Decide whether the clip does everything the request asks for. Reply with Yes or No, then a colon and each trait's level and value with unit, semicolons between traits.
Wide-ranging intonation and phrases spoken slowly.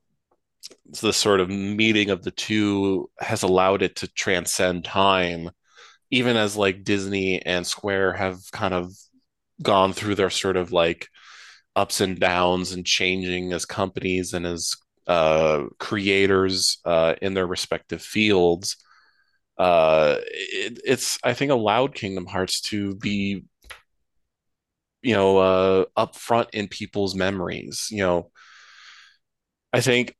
No: narrow, 2.4 semitones; slow, 130 wpm